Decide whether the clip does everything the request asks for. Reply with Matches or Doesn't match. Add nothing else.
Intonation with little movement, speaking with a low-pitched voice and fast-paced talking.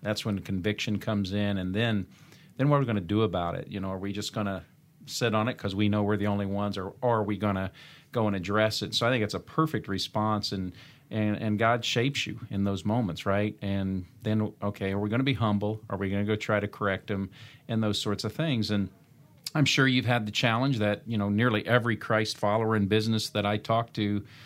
Matches